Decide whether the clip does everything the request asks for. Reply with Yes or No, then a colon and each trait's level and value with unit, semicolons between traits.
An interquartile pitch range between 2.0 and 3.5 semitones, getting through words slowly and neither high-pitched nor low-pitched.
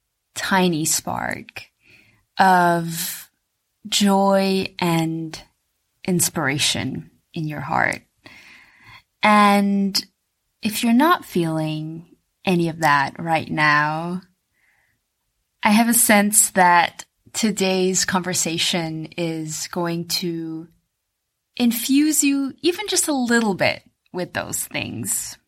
No: average, 4.5 semitones; slow, 90 wpm; medium, 175 Hz